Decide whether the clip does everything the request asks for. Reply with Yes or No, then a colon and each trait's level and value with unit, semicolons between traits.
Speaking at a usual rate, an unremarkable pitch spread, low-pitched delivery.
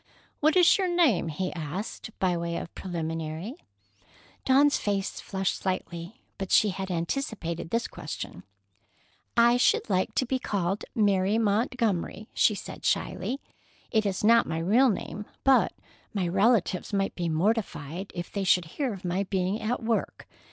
No: average, 150 wpm; average, 4.7 semitones; high, 195 Hz